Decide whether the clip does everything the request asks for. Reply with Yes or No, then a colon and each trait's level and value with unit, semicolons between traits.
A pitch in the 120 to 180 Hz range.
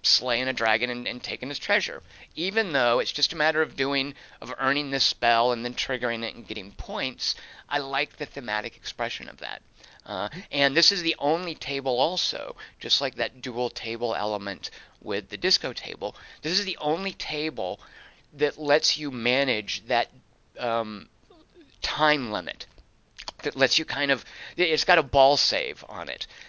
Yes: low, 135 Hz